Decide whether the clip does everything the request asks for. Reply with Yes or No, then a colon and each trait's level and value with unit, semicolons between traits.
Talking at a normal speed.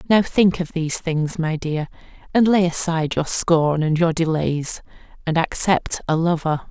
Yes: average, 170 wpm